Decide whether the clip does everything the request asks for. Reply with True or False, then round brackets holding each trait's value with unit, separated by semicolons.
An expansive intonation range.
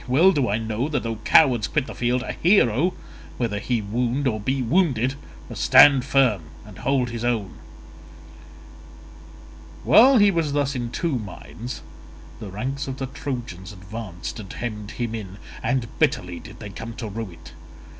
False (4.2 semitones)